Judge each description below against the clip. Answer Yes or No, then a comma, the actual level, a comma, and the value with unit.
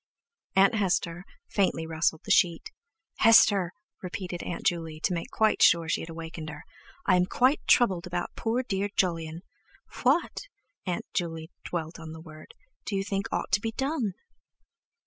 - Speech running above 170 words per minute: No, average, 165 wpm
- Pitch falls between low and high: Yes, medium, 180 Hz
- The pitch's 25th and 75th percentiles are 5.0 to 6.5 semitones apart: No, average, 3.8 semitones